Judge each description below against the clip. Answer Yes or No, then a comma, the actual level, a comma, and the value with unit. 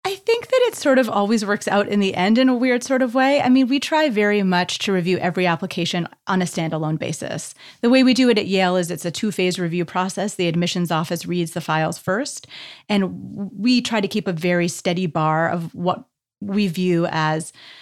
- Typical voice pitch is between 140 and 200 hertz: Yes, high, 190 Hz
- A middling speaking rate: No, fast, 225 wpm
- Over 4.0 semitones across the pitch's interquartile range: Yes, average, 5.0 semitones